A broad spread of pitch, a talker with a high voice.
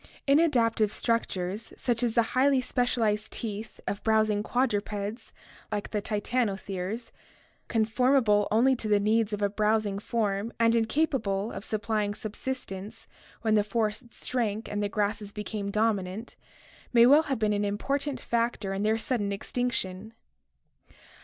No: narrow, 2.4 semitones; high, 215 Hz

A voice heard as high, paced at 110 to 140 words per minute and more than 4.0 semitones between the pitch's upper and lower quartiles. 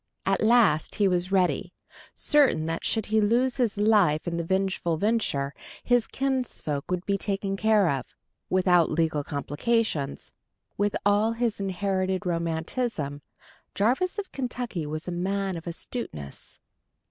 Yes: high, 195 Hz; slow, 135 wpm; average, 5.2 semitones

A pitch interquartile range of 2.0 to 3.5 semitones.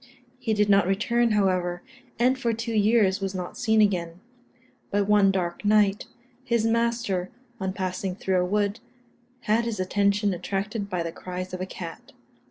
Yes: average, 3.0 semitones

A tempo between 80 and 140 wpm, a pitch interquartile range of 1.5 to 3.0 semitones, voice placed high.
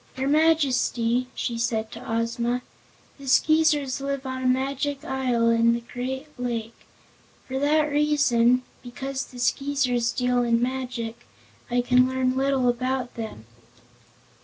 Yes: slow, 135 wpm; narrow, 2.4 semitones; very high, 255 Hz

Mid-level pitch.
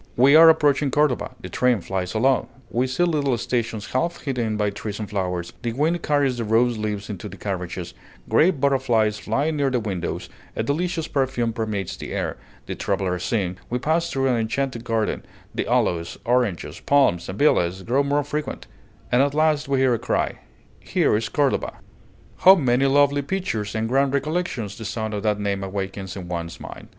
No: low, 120 Hz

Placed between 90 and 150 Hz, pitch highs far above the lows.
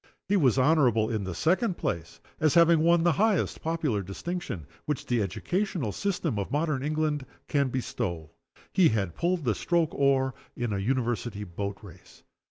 Yes: low, 135 Hz; wide, 7.9 semitones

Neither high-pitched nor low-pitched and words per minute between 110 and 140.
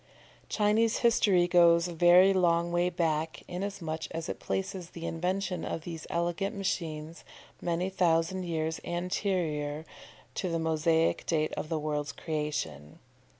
Yes: medium, 170 Hz; slow, 135 wpm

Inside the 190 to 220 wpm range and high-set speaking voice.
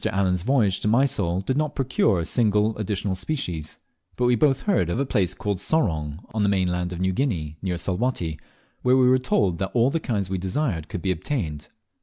No: fast, 205 wpm; low, 100 Hz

